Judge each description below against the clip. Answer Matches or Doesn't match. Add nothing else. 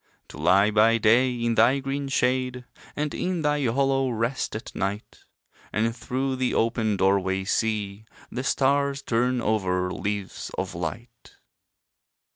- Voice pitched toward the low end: Matches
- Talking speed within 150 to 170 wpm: Doesn't match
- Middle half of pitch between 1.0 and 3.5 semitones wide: Doesn't match